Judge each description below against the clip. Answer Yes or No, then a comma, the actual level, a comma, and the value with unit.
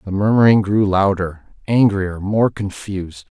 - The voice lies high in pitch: No, low, 100 Hz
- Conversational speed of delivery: No, slow, 125 wpm